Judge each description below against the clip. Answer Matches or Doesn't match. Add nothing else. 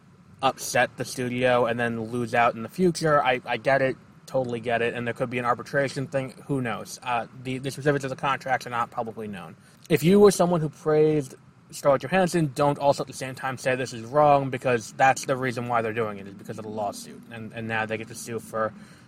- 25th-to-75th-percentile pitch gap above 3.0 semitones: Matches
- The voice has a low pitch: Matches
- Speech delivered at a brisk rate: Matches